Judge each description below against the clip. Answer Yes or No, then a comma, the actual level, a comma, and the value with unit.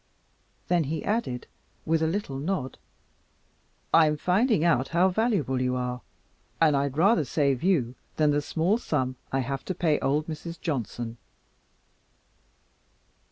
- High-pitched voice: No, medium, 155 Hz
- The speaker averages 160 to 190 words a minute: No, slow, 135 wpm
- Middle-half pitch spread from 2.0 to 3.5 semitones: No, average, 4.7 semitones